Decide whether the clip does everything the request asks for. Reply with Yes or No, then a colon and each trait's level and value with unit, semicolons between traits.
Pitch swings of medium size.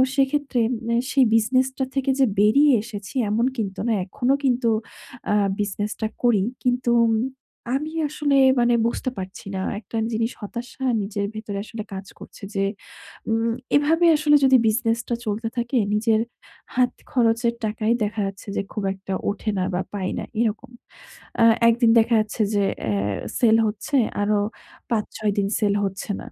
Yes: average, 3.2 semitones